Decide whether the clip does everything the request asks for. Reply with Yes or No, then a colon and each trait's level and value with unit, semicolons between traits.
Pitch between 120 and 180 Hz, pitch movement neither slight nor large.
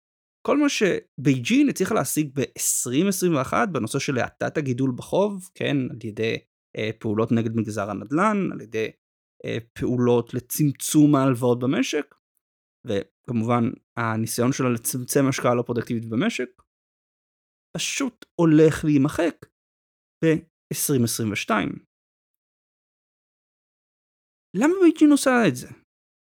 No: low, 135 Hz; wide, 5.7 semitones